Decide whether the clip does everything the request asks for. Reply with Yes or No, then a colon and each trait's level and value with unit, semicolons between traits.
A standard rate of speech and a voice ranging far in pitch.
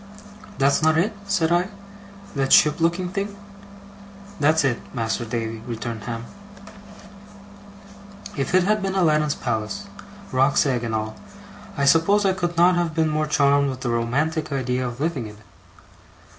Yes: average, 155 wpm; wide, 6.1 semitones